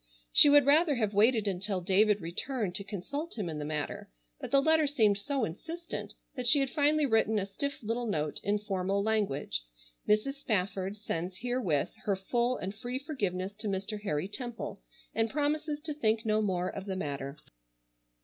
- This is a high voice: Yes, high, 215 Hz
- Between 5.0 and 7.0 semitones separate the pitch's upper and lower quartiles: Yes, wide, 5.6 semitones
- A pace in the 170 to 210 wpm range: Yes, average, 180 wpm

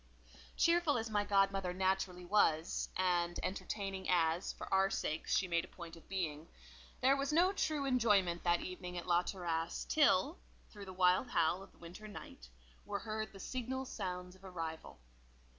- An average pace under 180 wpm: Yes, average, 170 wpm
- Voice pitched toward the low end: No, high, 190 Hz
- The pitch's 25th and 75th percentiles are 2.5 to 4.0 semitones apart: Yes, average, 3.6 semitones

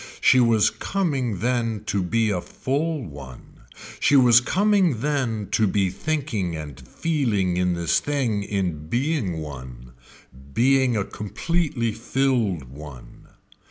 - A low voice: Yes, low, 110 Hz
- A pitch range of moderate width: No, wide, 7.3 semitones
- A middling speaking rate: No, slow, 125 wpm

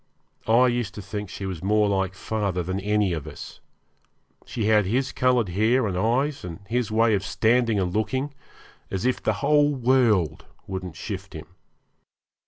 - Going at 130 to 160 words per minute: No, average, 170 wpm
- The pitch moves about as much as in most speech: Yes, average, 4.2 semitones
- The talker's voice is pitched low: Yes, low, 105 Hz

